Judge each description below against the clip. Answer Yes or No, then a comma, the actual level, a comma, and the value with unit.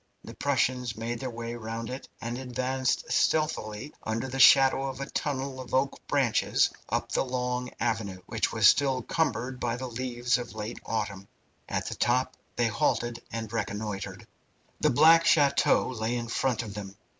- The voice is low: Yes, low, 120 Hz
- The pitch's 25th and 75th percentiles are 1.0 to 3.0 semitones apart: Yes, narrow, 2.5 semitones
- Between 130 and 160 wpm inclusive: No, average, 170 wpm